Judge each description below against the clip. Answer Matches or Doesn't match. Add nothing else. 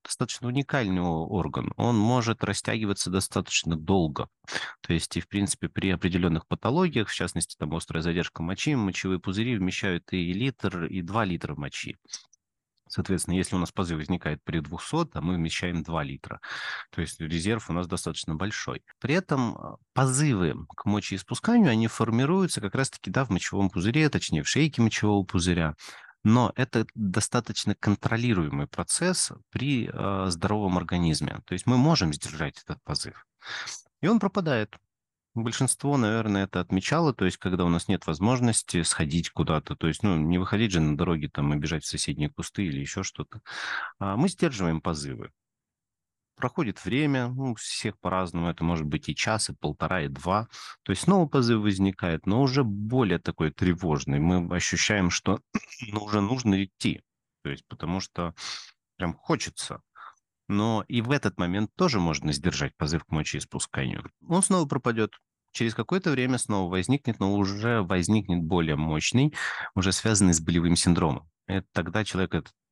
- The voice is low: Matches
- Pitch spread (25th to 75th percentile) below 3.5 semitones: Doesn't match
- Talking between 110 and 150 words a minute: Doesn't match